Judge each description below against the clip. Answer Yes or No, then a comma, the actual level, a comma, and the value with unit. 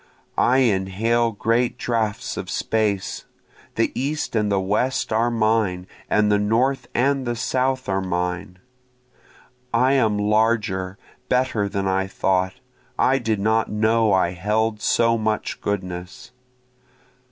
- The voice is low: Yes, low, 110 Hz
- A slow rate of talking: Yes, slow, 130 wpm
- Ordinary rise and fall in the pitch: Yes, average, 3.4 semitones